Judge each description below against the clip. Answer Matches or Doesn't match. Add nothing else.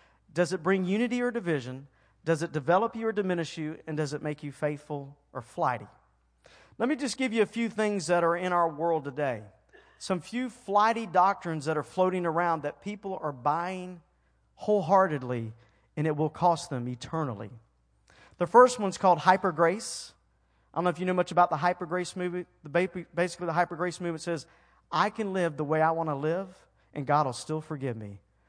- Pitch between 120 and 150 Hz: Doesn't match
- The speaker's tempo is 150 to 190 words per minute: Doesn't match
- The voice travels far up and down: Doesn't match